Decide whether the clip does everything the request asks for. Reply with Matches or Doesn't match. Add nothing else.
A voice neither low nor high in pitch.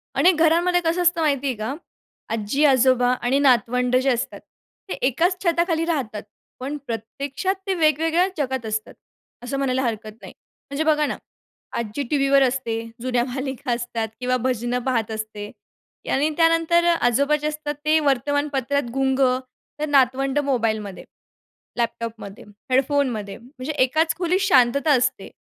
Doesn't match